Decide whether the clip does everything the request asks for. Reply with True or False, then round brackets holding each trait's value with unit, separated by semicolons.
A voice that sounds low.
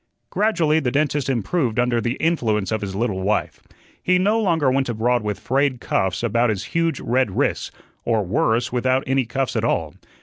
True (125 Hz)